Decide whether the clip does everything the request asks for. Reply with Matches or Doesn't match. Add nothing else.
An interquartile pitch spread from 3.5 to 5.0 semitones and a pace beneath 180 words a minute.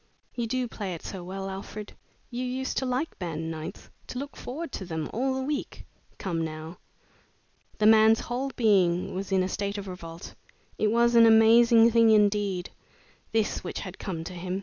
Doesn't match